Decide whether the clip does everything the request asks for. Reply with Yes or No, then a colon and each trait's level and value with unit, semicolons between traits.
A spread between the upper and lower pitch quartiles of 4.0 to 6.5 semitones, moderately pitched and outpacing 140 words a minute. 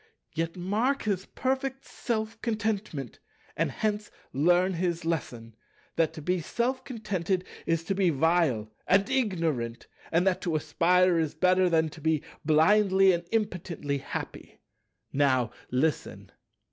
No: average, 4.6 semitones; medium, 175 Hz; slow, 135 wpm